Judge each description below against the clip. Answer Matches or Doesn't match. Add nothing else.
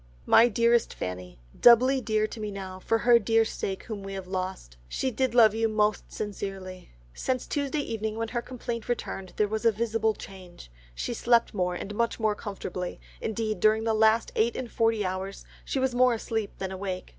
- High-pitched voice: Matches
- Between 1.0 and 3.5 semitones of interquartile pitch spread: Matches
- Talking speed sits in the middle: Matches